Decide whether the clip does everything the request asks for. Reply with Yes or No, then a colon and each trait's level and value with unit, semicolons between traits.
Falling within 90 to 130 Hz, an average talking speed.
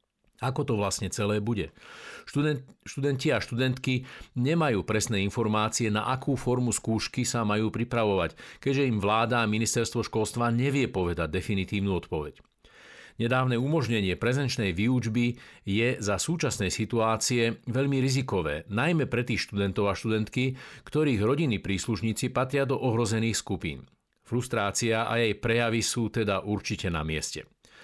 Yes: low, 115 Hz; average, 130 wpm